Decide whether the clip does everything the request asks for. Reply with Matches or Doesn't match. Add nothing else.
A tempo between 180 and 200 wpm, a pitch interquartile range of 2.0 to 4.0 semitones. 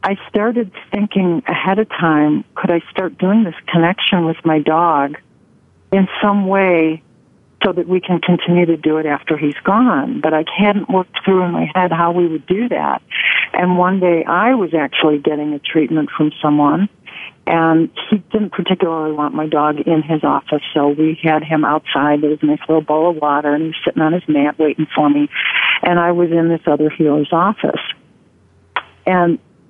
Matches